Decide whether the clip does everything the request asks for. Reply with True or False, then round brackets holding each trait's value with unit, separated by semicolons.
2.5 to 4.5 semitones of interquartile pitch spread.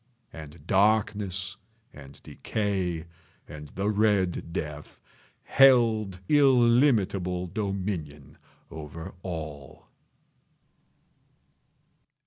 False (5.1 semitones)